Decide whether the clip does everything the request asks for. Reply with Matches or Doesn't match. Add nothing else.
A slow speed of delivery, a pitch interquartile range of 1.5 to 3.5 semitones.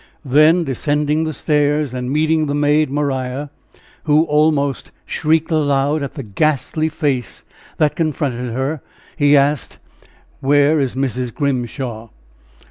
Matches